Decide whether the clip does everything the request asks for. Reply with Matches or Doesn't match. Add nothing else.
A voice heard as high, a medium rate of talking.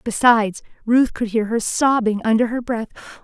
Matches